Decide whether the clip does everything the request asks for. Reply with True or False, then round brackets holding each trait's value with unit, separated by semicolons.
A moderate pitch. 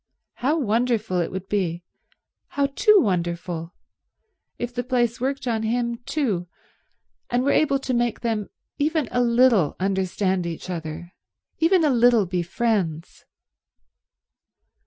False (230 Hz)